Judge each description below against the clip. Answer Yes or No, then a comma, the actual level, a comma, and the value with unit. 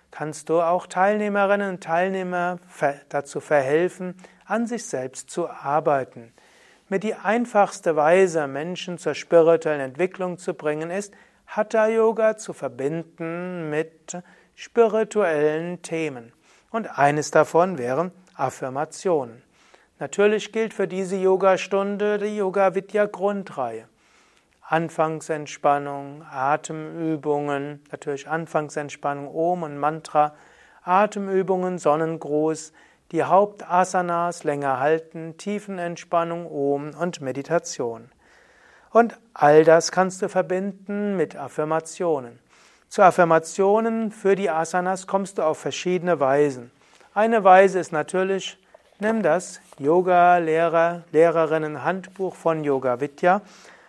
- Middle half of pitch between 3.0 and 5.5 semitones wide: Yes, average, 4.1 semitones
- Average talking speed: No, slow, 100 wpm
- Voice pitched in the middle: Yes, medium, 170 Hz